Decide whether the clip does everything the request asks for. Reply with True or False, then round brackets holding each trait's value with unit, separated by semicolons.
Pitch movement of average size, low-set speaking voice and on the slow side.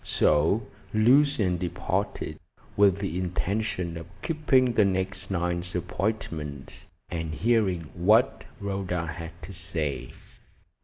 True (4.1 semitones; 90 Hz; 105 wpm)